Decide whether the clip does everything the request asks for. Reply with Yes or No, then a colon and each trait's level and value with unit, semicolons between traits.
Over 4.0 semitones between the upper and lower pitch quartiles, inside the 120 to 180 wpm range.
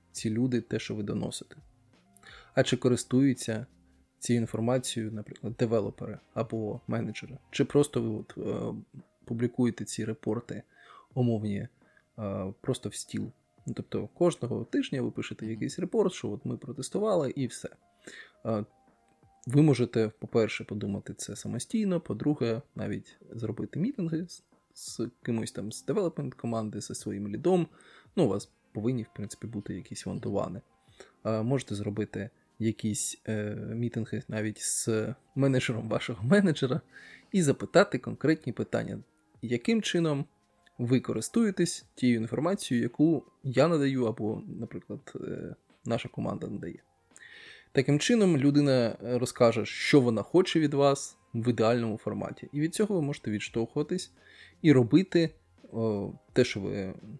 Yes: average, 4.5 semitones; average, 125 wpm